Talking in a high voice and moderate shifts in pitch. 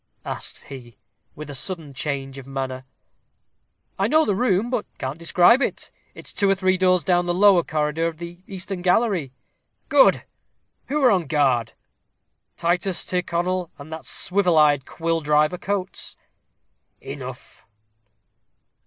No: medium, 175 Hz; average, 4.0 semitones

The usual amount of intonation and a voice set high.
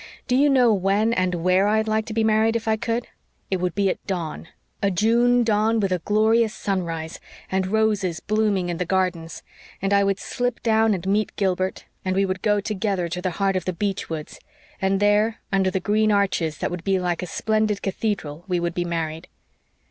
Yes: average, 3.1 semitones; high, 195 Hz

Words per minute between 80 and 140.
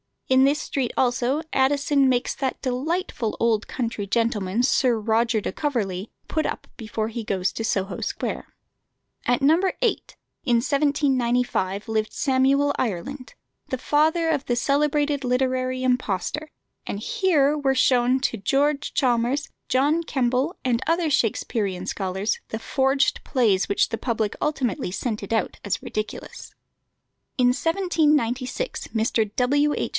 Yes: slow, 135 wpm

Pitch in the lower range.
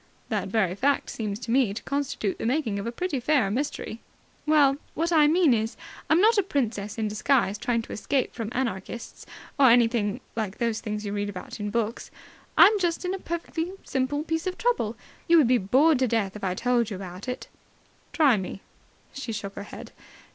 No: high, 240 Hz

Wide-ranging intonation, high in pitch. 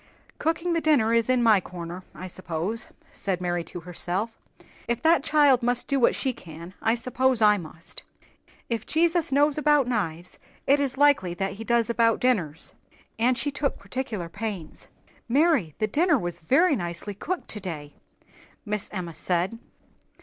Yes: wide, 7.2 semitones; high, 225 Hz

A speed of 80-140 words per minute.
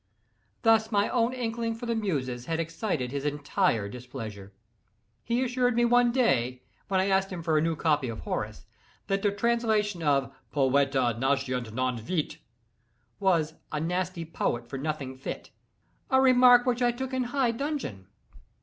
No: average, 160 wpm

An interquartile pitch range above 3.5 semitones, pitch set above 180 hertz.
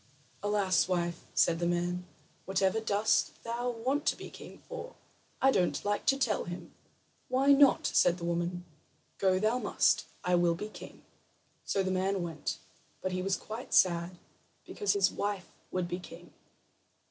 Yes: average, 3.9 semitones; high, 190 Hz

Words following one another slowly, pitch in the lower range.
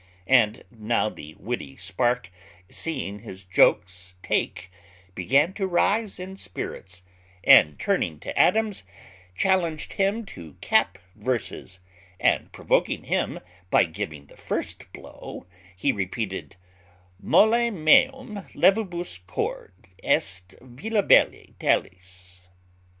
Yes: slow, 105 wpm; low, 110 Hz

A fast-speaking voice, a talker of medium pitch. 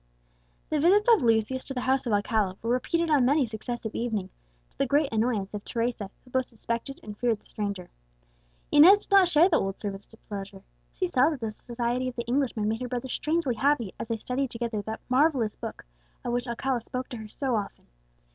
No: fast, 210 wpm; high, 240 Hz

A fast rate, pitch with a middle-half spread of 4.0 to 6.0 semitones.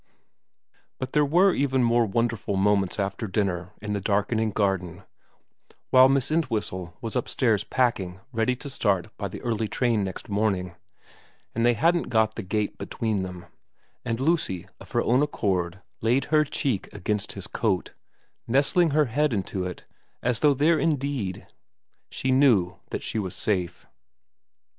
No: average, 150 wpm; average, 5.1 semitones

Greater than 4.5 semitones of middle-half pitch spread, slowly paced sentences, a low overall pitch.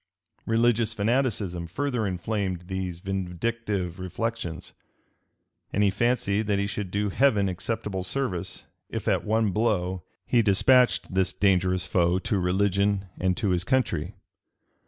No: average, 3.5 semitones; slow, 130 wpm; low, 100 Hz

